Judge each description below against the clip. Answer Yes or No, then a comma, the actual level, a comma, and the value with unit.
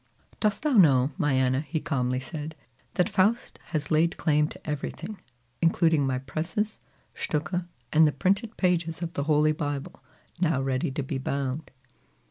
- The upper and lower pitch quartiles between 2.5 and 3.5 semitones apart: No, average, 3.9 semitones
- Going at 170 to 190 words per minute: No, average, 155 wpm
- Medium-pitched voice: Yes, medium, 155 Hz